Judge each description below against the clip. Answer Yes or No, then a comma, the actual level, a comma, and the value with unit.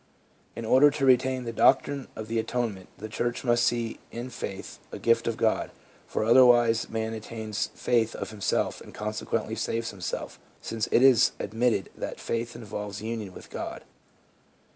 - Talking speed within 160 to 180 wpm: Yes, average, 165 wpm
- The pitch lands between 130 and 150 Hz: No, low, 115 Hz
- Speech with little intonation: Yes, narrow, 1.7 semitones